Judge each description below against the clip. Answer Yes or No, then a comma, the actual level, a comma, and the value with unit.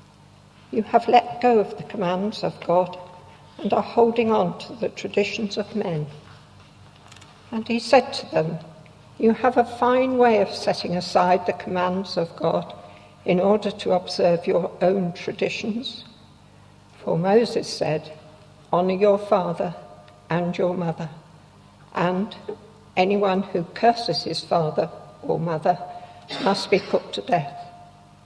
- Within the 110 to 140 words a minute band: Yes, slow, 135 wpm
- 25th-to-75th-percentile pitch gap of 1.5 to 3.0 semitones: No, average, 4.1 semitones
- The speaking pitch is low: No, medium, 185 Hz